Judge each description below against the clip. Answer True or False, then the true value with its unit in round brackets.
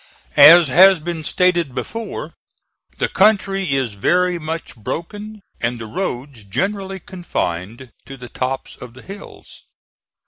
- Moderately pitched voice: True (165 Hz)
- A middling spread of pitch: False (7.3 semitones)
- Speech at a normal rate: False (130 wpm)